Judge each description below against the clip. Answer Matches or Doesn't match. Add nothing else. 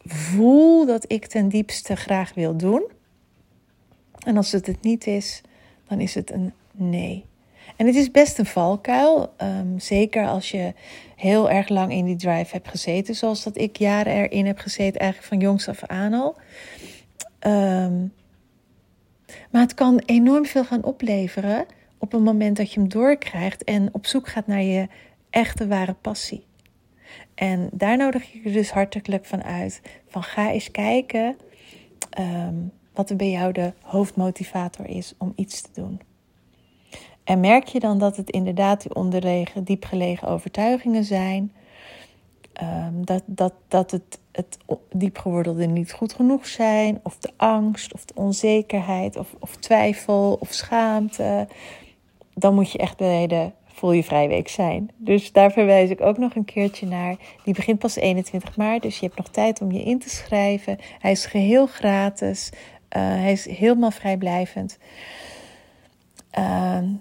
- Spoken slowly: Doesn't match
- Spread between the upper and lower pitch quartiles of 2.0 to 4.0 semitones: Matches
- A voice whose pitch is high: Matches